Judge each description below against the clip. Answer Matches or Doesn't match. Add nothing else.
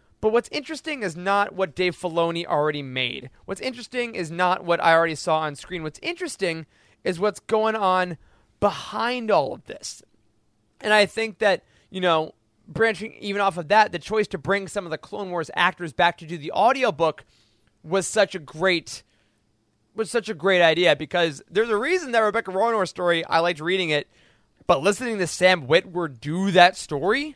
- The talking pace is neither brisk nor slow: Matches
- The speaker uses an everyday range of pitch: Matches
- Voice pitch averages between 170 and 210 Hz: Matches